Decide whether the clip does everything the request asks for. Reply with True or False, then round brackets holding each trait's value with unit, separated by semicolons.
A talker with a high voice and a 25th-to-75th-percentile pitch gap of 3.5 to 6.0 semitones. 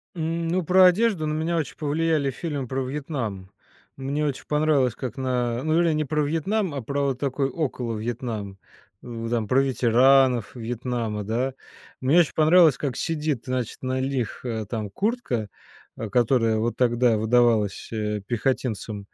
False (130 Hz; 4.7 semitones)